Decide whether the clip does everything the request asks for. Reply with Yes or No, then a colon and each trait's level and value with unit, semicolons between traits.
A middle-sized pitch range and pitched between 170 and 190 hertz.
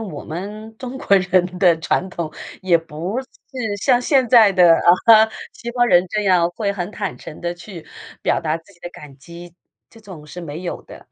Yes: average, 4.4 semitones; medium, 185 Hz